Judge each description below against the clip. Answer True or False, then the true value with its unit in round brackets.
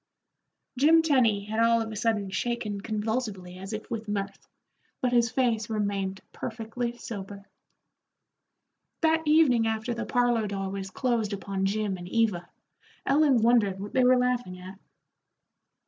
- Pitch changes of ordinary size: True (3.5 semitones)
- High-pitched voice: True (220 Hz)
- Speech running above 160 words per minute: False (145 wpm)